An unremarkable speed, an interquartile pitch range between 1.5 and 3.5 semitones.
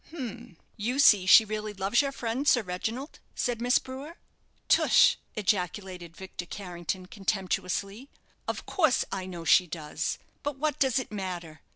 No: average, 155 wpm; wide, 5.5 semitones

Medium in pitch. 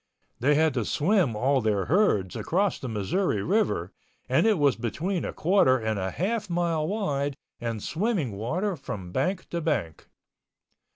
Yes: medium, 150 Hz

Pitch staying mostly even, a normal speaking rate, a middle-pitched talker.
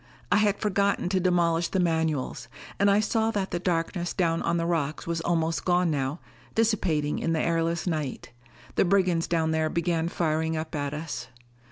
Yes: narrow, 2.3 semitones; average, 180 wpm; medium, 170 Hz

